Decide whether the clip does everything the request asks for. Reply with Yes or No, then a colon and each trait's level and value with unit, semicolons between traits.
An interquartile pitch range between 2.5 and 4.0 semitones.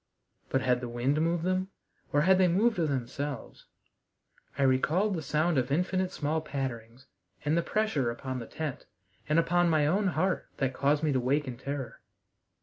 No: average, 5.0 semitones